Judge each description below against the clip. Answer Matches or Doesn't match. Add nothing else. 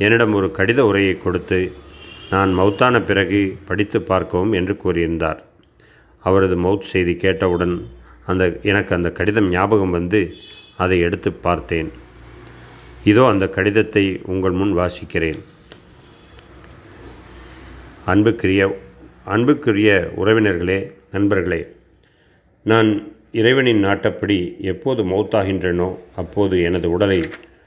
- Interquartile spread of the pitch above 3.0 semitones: Doesn't match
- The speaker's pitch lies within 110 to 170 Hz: Doesn't match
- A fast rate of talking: Doesn't match